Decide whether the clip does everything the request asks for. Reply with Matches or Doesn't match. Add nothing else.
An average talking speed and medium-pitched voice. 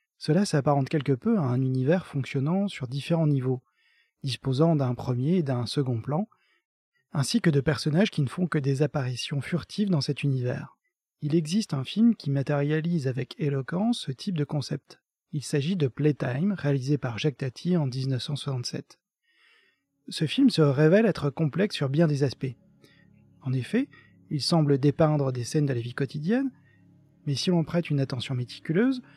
Matches